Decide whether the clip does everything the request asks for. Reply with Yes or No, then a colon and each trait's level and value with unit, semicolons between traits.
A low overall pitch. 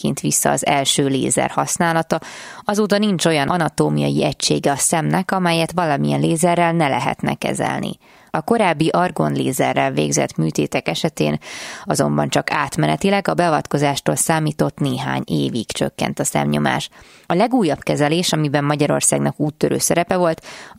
No: medium, 150 Hz